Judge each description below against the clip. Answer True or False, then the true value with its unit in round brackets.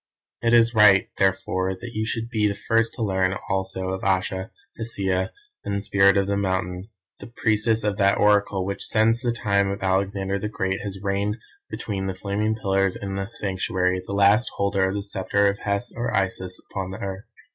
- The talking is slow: False (190 wpm)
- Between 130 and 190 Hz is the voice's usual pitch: False (100 Hz)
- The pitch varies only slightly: True (1.8 semitones)